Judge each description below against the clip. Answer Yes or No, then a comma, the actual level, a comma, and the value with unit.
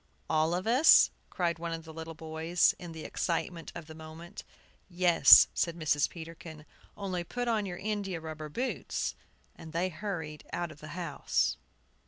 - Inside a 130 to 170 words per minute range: Yes, average, 165 wpm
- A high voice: No, medium, 165 Hz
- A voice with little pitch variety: Yes, narrow, 2.3 semitones